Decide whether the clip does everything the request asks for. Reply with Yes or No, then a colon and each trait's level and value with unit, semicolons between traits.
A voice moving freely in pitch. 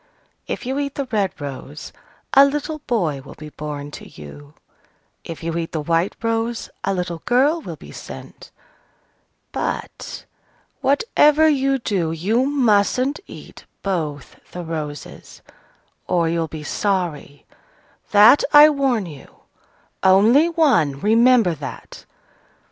Yes: wide, 8.8 semitones